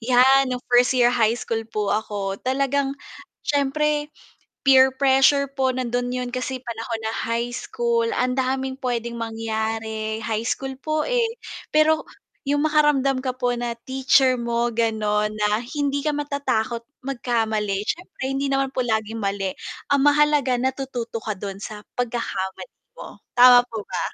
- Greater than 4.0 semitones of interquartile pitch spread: No, average, 3.4 semitones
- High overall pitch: Yes, very high, 250 Hz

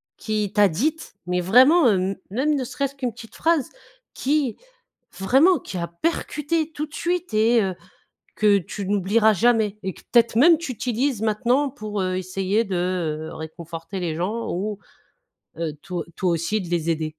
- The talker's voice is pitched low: No, high, 210 Hz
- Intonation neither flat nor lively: No, wide, 6.1 semitones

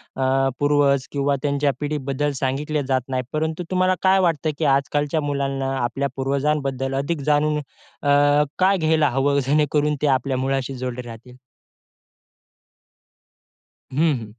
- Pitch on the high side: No, medium, 140 Hz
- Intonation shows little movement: Yes, narrow, 2.0 semitones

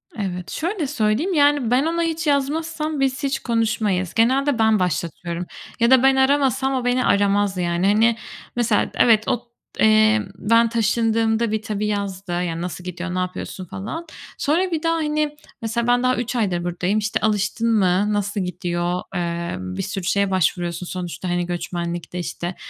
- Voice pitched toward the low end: No, high, 215 Hz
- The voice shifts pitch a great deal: Yes, wide, 6.0 semitones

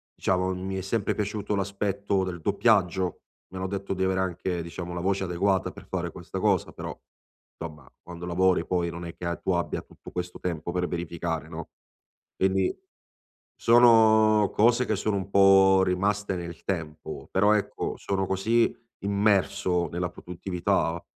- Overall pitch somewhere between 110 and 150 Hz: No, very low, 95 Hz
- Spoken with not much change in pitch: Yes, narrow, 2.3 semitones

